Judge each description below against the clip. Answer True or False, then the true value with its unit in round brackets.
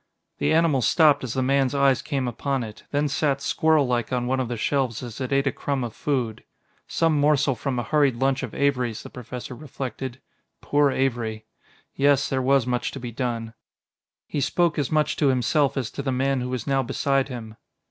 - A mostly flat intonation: True (2.3 semitones)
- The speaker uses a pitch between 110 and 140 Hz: True (135 Hz)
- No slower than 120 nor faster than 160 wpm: False (200 wpm)